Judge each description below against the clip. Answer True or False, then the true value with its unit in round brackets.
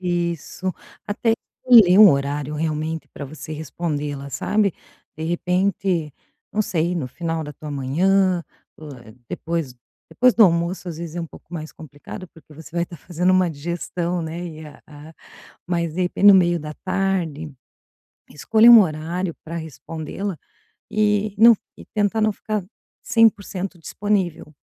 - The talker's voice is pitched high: False (170 Hz)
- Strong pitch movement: False (3.7 semitones)